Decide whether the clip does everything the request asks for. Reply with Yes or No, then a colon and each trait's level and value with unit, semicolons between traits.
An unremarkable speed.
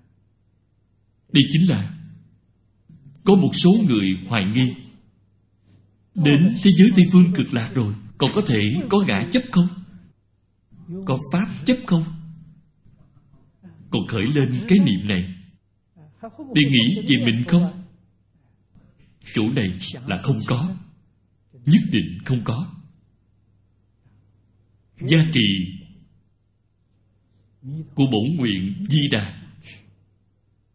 No: slow, 105 wpm